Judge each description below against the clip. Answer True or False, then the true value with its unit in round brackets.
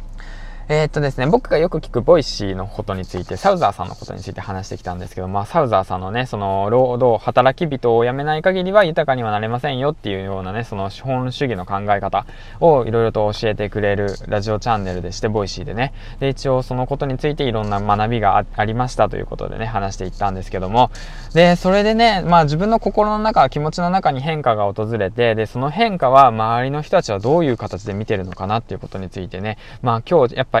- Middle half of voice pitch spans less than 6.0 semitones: True (5.5 semitones)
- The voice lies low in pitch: True (115 Hz)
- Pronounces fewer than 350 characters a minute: False (470 characters per minute)